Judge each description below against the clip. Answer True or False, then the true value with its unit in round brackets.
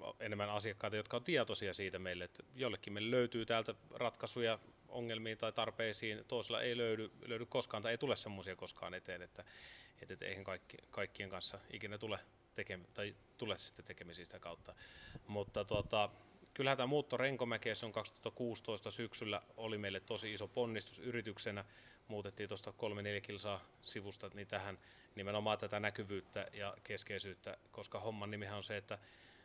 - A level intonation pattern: True (2.3 semitones)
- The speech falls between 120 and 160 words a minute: True (155 wpm)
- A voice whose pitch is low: True (105 Hz)